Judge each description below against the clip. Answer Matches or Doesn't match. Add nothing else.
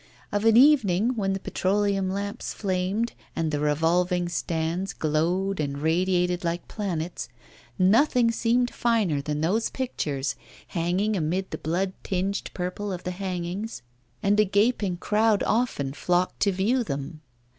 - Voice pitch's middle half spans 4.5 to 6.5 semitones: Doesn't match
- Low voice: Doesn't match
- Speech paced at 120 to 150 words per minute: Matches